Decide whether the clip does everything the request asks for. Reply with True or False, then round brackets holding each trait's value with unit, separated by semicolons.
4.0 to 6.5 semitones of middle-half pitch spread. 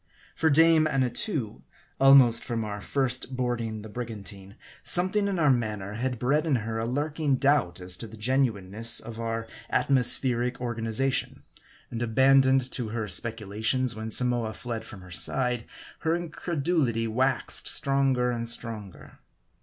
False (3.4 semitones)